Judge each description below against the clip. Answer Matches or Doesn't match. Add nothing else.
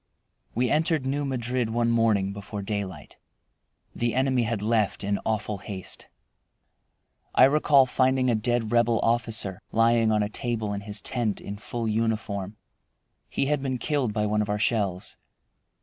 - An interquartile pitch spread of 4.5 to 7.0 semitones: Doesn't match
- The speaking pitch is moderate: Doesn't match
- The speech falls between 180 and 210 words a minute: Doesn't match